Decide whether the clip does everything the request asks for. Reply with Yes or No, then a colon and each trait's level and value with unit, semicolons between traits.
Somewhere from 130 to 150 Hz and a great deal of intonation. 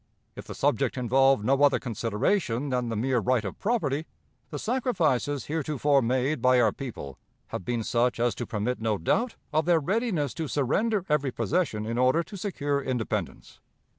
No: low, 135 Hz; average, 4.8 semitones